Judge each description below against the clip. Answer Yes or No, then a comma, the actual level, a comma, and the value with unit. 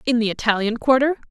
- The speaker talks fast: No, average, 185 wpm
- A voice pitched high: Yes, high, 240 Hz